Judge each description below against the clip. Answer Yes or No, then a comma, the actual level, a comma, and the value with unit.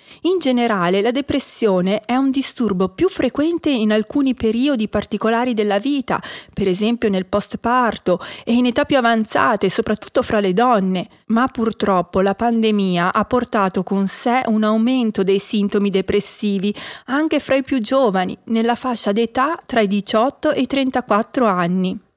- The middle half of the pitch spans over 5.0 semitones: No, average, 4.0 semitones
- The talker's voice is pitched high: Yes, high, 225 Hz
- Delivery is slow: No, average, 155 wpm